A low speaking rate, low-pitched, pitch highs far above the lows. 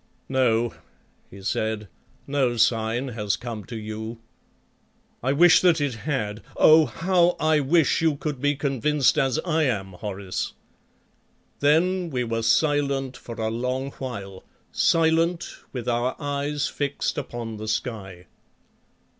No: slow, 130 wpm; low, 130 Hz; average, 4.8 semitones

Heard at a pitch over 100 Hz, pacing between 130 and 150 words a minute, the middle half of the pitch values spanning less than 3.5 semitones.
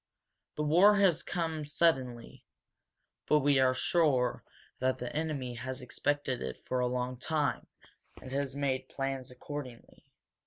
Yes: low, 135 Hz; average, 140 wpm; average, 3.0 semitones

